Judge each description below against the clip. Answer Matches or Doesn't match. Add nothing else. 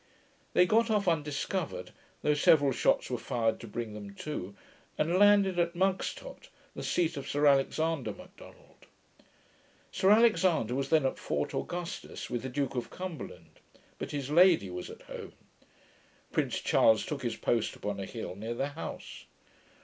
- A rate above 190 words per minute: Doesn't match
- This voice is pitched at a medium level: Matches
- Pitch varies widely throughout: Matches